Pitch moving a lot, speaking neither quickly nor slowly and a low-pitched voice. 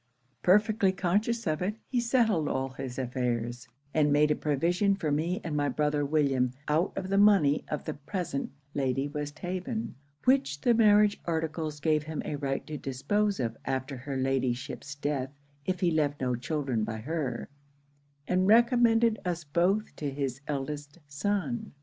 No: wide, 6.0 semitones; average, 160 wpm; medium, 150 Hz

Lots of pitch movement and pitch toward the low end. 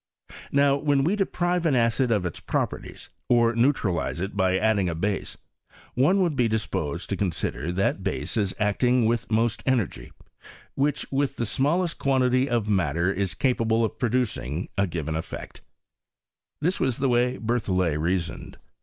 Yes: wide, 5.9 semitones; low, 115 Hz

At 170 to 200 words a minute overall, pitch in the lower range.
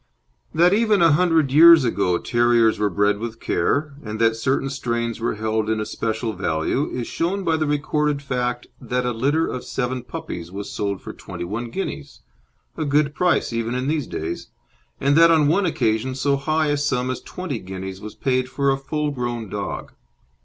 Yes: average, 190 wpm; low, 125 Hz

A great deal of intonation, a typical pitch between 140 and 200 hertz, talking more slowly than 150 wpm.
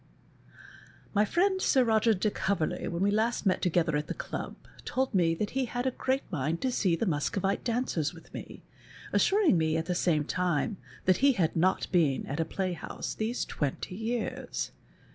No: wide, 6.1 semitones; high, 190 Hz; average, 180 wpm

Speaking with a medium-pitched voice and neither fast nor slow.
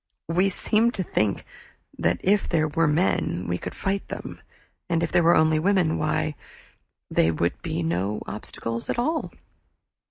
Yes: medium, 160 Hz; average, 160 wpm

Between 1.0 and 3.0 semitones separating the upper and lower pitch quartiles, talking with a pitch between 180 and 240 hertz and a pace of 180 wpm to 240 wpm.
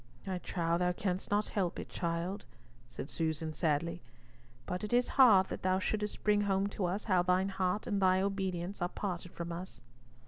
Yes: narrow, 2.6 semitones; medium, 185 Hz; average, 185 wpm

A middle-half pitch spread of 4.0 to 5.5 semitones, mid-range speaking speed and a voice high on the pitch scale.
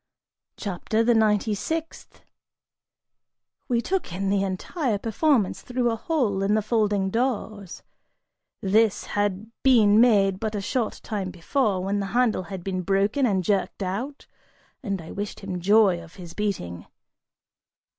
No: average, 3.0 semitones; average, 145 wpm; high, 205 Hz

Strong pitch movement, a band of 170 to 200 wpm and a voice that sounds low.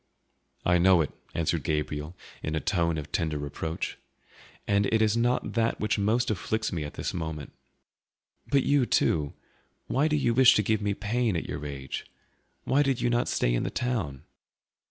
Yes: wide, 7.2 semitones; average, 180 wpm; very low, 95 Hz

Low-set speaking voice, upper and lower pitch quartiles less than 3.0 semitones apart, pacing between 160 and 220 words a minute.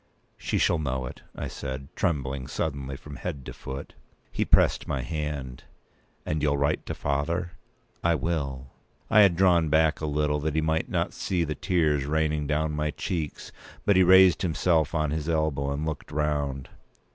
Yes: very low, 75 Hz; narrow, 2.4 semitones; average, 175 wpm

